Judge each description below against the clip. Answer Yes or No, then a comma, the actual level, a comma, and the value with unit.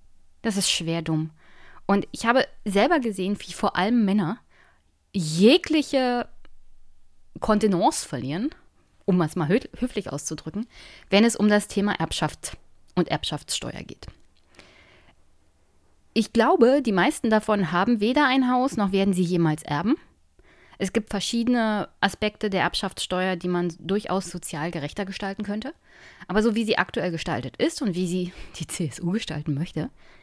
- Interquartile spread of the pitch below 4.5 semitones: No, average, 5.2 semitones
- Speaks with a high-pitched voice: Yes, high, 195 Hz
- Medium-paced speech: Yes, average, 140 wpm